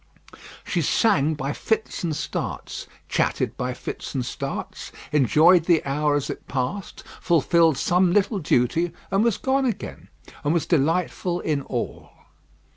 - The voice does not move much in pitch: No, average, 4.4 semitones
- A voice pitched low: No, medium, 165 Hz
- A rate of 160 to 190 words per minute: No, average, 140 wpm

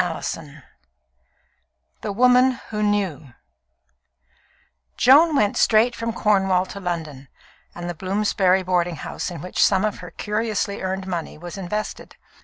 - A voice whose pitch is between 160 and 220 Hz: Yes, high, 190 Hz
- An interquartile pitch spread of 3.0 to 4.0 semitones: Yes, average, 3.4 semitones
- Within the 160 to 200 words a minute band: No, slow, 135 wpm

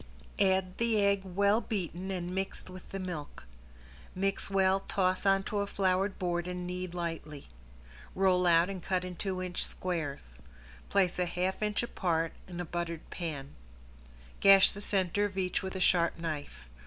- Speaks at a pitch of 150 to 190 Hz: Yes, medium, 185 Hz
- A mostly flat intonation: Yes, narrow, 2.0 semitones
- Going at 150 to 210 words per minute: Yes, average, 165 wpm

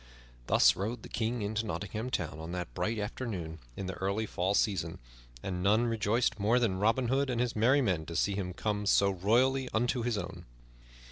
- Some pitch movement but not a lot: Yes, average, 4.0 semitones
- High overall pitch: No, low, 105 Hz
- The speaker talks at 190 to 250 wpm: Yes, average, 195 wpm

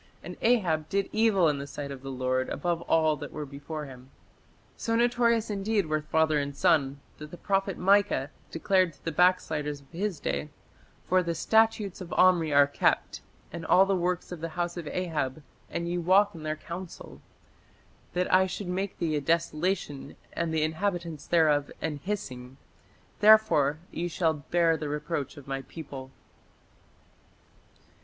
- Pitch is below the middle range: No, medium, 165 Hz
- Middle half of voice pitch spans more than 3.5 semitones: Yes, average, 3.9 semitones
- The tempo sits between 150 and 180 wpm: Yes, average, 165 wpm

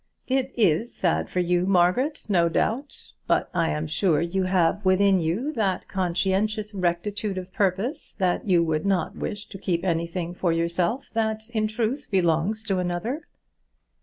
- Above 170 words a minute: No, average, 160 wpm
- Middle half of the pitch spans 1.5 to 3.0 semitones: No, average, 3.8 semitones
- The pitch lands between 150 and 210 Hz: Yes, high, 190 Hz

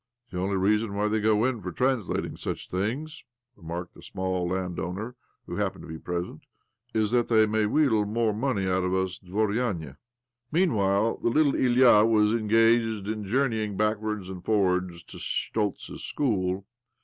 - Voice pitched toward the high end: No, low, 105 Hz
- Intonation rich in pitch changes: No, average, 3.4 semitones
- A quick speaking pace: No, average, 175 wpm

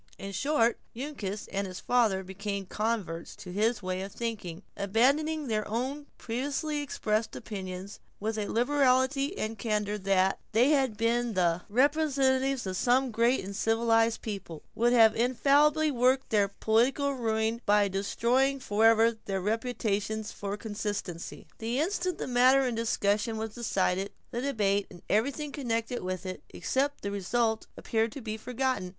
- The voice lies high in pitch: Yes, high, 225 Hz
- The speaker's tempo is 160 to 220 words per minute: No, average, 150 wpm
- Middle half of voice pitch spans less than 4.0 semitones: No, average, 4.3 semitones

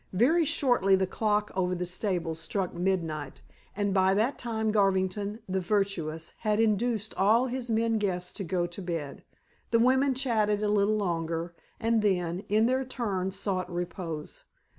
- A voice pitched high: Yes, high, 200 Hz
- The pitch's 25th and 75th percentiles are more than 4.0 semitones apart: No, average, 3.7 semitones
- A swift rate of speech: No, average, 160 wpm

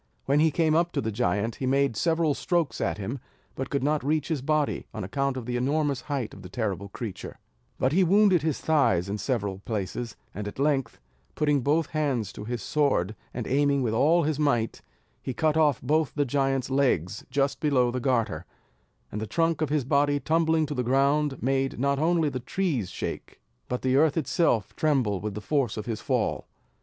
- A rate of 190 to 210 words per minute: Yes, average, 200 wpm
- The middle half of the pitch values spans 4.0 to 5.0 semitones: Yes, average, 4.4 semitones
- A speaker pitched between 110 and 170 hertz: Yes, low, 135 Hz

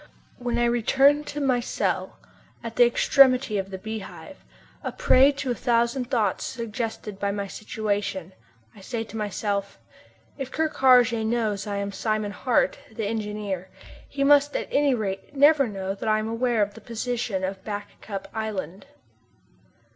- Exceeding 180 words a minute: No, average, 160 wpm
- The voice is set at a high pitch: Yes, high, 225 Hz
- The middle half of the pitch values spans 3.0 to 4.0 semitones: Yes, average, 3.6 semitones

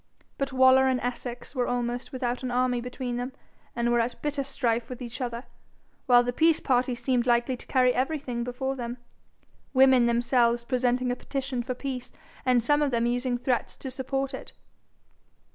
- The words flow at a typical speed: Yes, average, 180 wpm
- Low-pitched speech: No, very high, 250 Hz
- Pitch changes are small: Yes, narrow, 1.5 semitones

